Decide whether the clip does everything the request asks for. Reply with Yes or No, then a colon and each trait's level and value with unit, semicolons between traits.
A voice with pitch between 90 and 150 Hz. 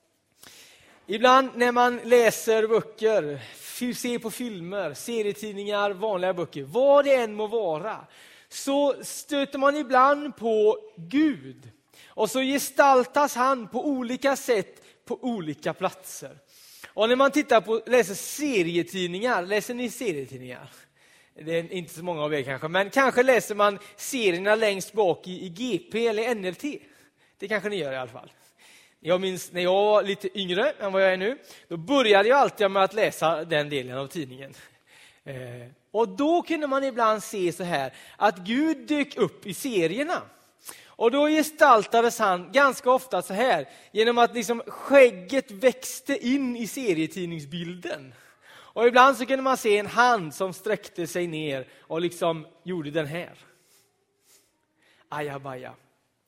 No: high, 215 Hz